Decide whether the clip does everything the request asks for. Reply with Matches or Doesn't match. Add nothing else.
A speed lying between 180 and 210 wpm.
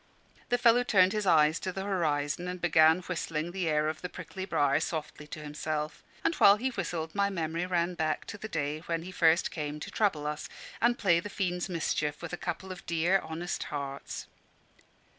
Matches